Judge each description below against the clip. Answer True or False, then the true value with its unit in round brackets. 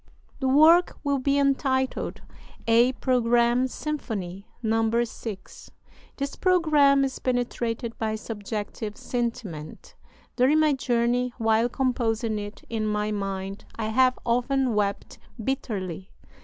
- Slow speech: True (115 wpm)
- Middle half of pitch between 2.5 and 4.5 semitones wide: True (3.5 semitones)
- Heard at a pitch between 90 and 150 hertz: False (235 Hz)